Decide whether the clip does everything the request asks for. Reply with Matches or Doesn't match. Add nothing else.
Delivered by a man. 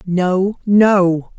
Doesn't match